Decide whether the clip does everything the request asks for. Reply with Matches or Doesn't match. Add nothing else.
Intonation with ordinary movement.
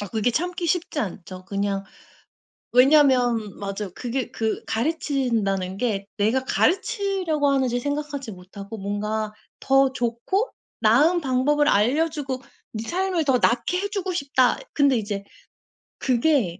Doesn't match